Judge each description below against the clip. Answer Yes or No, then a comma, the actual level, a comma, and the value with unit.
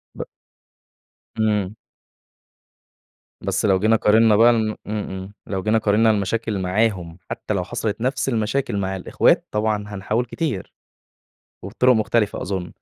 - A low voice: Yes, low, 105 Hz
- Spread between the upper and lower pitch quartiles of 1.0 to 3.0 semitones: Yes, narrow, 2.6 semitones